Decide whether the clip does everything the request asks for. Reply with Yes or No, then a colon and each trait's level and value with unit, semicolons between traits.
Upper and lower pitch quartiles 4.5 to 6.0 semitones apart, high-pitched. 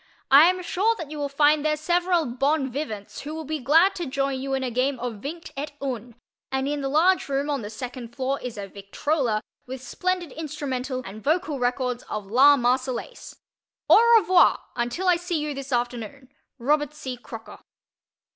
No: average, 3.8 semitones; very high, 275 Hz